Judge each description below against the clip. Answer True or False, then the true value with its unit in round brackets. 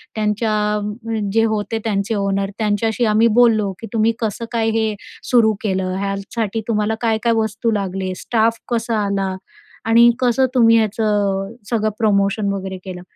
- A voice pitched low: False (215 Hz)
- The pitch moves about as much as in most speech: False (2.2 semitones)